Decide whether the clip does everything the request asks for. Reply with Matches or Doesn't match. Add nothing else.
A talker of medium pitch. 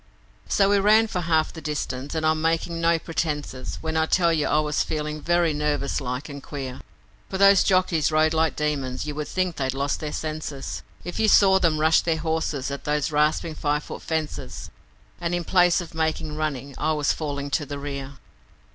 Matches